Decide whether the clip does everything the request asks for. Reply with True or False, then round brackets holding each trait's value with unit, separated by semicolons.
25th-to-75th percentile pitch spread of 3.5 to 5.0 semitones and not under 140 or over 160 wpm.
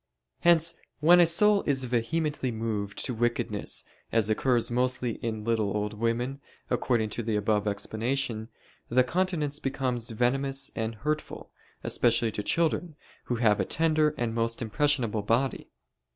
True (4.5 semitones; 145 wpm)